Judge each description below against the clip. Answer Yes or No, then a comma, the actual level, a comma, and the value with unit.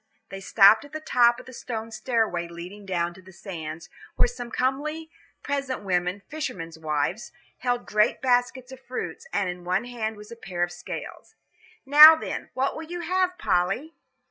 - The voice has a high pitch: Yes, high, 230 Hz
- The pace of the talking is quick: No, average, 175 wpm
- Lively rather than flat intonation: Yes, wide, 6.5 semitones